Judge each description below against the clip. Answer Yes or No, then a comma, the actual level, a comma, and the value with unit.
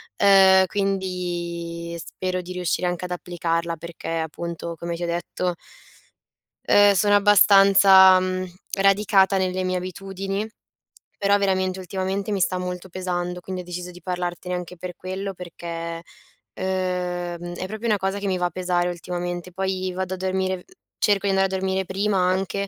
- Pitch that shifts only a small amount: Yes, narrow, 1.5 semitones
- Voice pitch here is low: No, medium, 185 Hz